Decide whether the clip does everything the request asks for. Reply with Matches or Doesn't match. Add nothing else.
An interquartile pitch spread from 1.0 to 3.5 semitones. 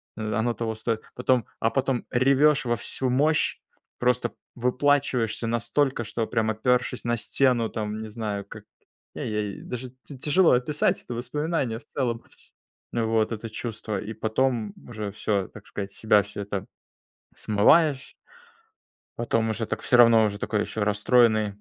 Matches